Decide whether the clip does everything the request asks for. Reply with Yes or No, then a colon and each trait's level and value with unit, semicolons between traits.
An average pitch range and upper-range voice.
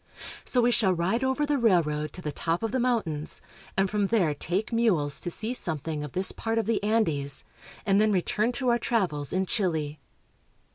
No: wide, 6.3 semitones; high, 195 Hz